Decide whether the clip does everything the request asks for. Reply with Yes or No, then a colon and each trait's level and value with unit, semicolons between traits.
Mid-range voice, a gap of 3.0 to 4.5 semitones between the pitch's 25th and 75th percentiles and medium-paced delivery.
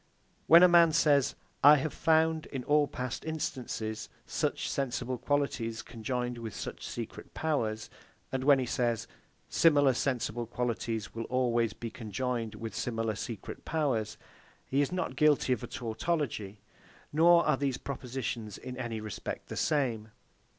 No: low, 125 Hz; average, 4.2 semitones; average, 145 wpm